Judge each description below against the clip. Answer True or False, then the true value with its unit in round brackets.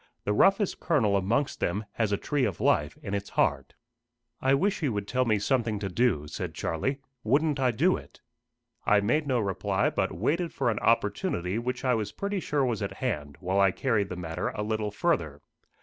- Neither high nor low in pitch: False (110 Hz)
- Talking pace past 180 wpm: True (200 wpm)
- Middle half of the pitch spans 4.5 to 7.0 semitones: True (5.2 semitones)